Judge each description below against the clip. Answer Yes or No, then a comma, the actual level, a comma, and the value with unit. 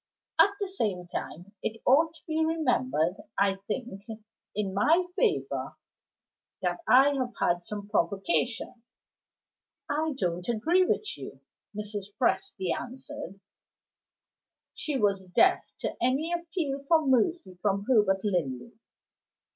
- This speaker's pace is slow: Yes, slow, 120 wpm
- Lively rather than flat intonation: Yes, wide, 8.1 semitones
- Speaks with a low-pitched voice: No, high, 240 Hz